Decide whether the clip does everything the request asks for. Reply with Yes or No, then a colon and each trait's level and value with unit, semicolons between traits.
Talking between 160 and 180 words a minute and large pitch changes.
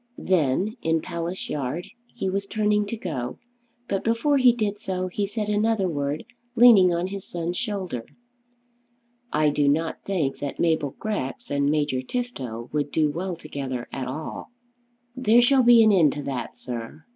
Yes: average, 165 wpm; wide, 6.5 semitones